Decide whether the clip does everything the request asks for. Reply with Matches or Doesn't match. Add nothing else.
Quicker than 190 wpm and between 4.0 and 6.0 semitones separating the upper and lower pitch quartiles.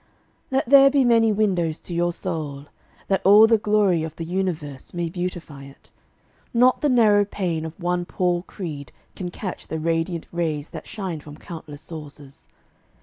Doesn't match